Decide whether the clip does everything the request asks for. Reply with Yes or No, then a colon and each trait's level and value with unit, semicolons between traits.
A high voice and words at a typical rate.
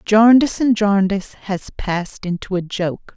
Yes: high, 200 Hz; average, 150 wpm